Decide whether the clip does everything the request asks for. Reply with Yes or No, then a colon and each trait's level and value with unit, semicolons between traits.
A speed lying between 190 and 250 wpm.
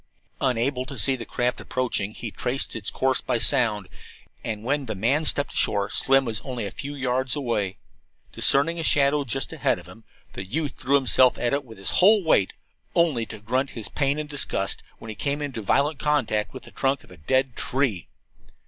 Yes: average, 200 wpm